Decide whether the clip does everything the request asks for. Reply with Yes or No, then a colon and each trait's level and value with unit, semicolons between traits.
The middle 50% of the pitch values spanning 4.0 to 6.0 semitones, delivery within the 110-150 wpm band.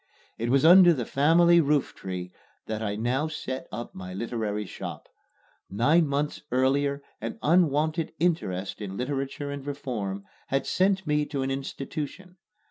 Yes: average, 5.3 semitones; average, 140 wpm